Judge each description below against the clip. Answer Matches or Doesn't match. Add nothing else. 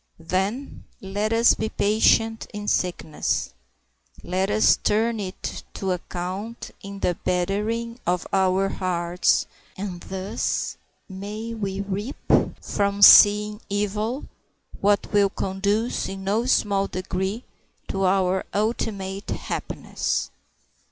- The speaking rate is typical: Doesn't match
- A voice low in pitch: Doesn't match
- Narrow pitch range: Matches